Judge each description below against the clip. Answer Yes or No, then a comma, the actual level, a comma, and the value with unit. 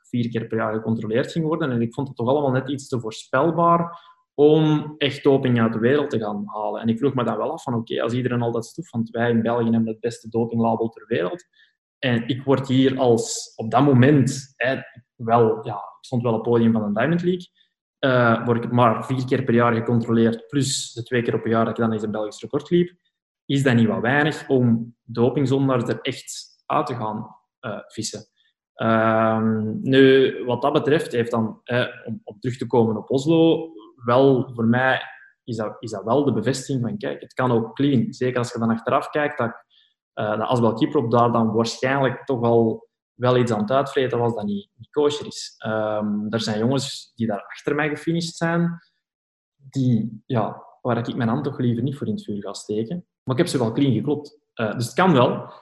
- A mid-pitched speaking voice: No, low, 120 Hz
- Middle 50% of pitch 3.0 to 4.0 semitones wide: Yes, average, 3.7 semitones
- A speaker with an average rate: No, fast, 220 wpm